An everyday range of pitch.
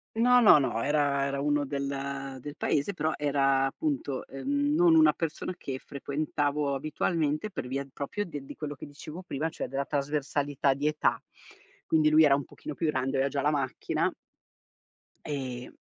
No: narrow, 2.0 semitones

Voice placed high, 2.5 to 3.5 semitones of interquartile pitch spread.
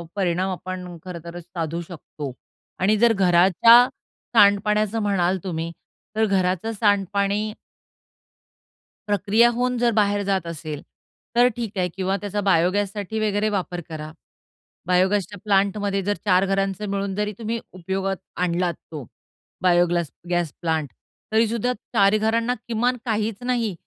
Yes: high, 195 Hz; average, 3.0 semitones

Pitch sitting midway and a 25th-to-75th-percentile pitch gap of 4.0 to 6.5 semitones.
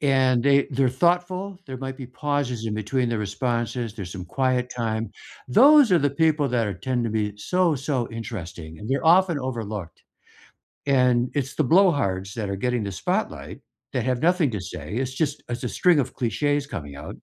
No: low, 125 Hz; average, 4.7 semitones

